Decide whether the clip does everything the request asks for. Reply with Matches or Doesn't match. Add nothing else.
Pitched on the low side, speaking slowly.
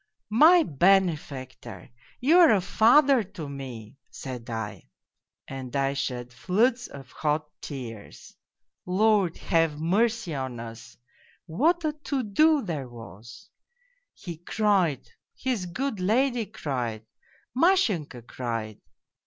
Doesn't match